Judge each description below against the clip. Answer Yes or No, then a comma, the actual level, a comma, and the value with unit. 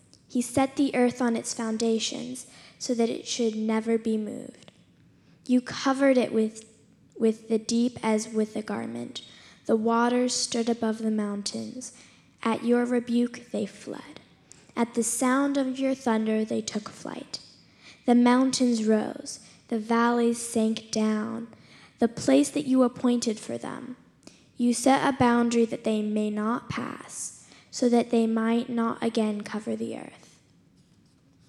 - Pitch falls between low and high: No, high, 235 Hz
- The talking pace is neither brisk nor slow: Yes, average, 145 wpm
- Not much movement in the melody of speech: Yes, narrow, 2.0 semitones